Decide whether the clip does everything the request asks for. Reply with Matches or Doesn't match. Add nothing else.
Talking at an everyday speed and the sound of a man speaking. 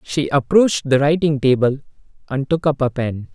Matches